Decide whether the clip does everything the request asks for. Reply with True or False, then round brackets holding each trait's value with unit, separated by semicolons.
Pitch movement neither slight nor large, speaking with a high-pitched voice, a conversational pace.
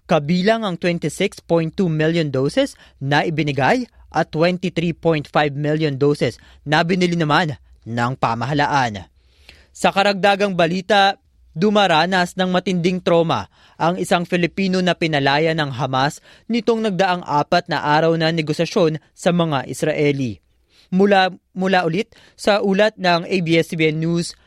False (4.0 semitones; 165 Hz; 120 wpm)